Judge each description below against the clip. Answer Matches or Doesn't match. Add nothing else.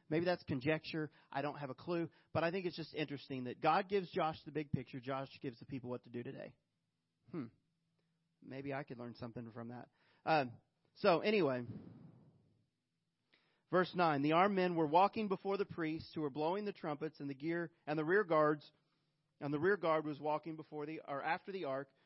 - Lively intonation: Doesn't match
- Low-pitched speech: Doesn't match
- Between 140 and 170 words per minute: Doesn't match